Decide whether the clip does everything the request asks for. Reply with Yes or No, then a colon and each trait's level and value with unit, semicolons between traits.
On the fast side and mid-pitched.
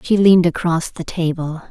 No: average, 175 wpm; medium, 170 Hz